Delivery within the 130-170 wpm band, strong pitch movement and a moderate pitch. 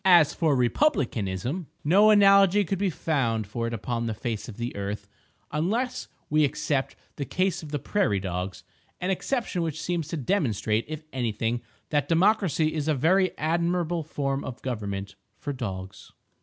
Yes: average, 155 wpm; wide, 7.3 semitones; medium, 145 Hz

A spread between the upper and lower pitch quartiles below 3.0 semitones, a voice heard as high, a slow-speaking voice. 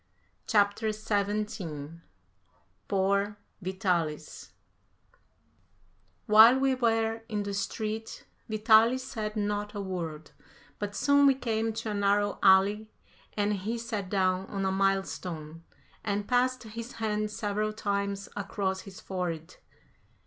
Yes: narrow, 2.4 semitones; high, 205 Hz; slow, 120 wpm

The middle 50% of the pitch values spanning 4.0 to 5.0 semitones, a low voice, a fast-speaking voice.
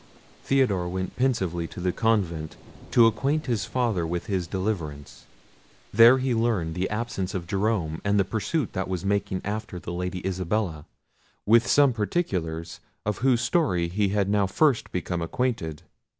No: average, 4.7 semitones; low, 100 Hz; average, 150 wpm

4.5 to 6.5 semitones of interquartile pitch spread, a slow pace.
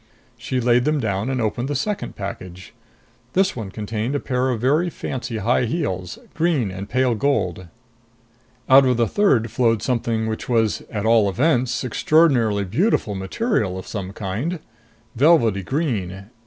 No: average, 4.9 semitones; average, 155 wpm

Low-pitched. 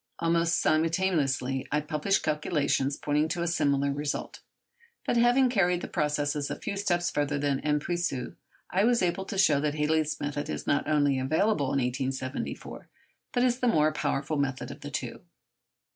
No: medium, 150 Hz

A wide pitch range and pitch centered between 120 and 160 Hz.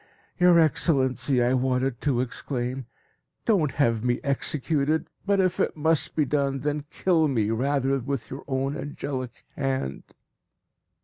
No: average, 2.9 semitones; low, 135 Hz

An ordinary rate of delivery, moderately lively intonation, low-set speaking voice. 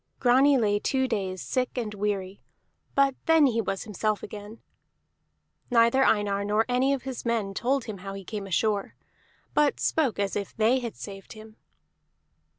No: average, 160 wpm; average, 4.0 semitones; high, 220 Hz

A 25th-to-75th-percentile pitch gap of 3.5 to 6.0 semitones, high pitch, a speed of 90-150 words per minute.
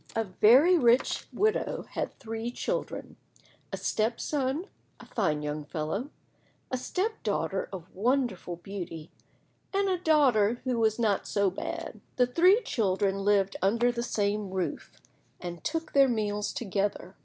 Yes: average, 5.2 semitones; high, 220 Hz; average, 145 wpm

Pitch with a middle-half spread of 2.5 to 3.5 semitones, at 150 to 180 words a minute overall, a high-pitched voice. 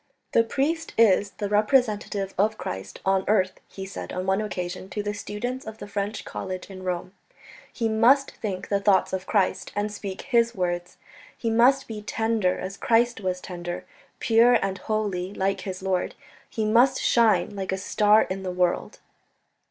Yes: average, 3.0 semitones; average, 175 wpm; high, 205 Hz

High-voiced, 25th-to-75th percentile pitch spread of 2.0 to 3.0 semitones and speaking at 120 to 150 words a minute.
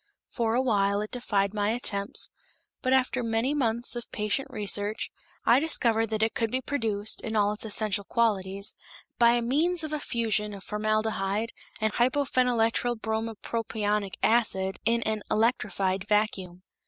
Yes: high, 220 Hz; narrow, 2.5 semitones; average, 140 wpm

